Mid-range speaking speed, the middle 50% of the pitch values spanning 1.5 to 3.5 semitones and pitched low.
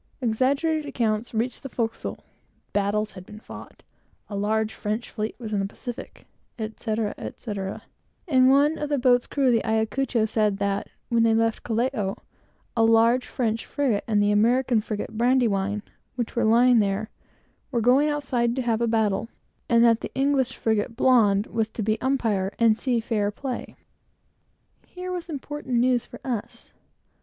No: average, 165 wpm; average, 2.9 semitones; high, 230 Hz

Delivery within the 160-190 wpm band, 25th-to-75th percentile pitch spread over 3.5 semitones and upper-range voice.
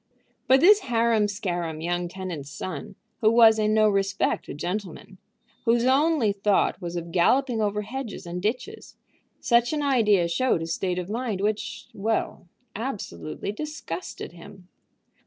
No: average, 145 wpm; average, 5.0 semitones; high, 210 Hz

